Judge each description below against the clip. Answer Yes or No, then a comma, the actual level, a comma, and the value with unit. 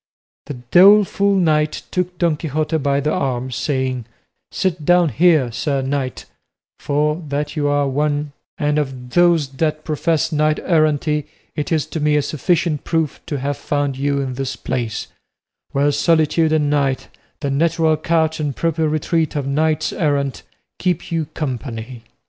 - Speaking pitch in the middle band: Yes, medium, 150 Hz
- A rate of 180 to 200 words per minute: No, average, 155 wpm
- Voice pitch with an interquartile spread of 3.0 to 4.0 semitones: No, narrow, 2.4 semitones